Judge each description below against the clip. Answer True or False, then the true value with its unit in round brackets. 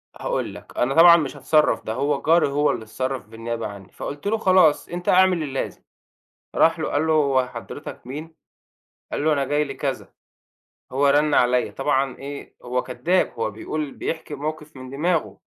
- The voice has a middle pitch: True (145 Hz)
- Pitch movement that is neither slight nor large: True (3.5 semitones)